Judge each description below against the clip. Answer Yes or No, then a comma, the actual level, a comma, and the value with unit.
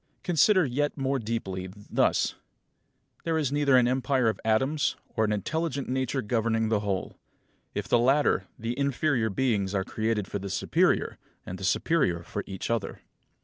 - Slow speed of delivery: No, average, 160 wpm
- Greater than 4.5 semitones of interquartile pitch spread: Yes, average, 5.1 semitones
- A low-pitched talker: Yes, low, 115 Hz